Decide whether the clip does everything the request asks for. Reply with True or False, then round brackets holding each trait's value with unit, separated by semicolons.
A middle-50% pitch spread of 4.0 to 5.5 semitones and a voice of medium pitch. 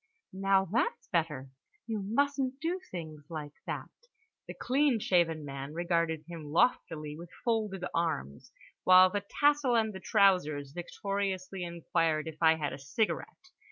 True (5.2 semitones; 175 Hz)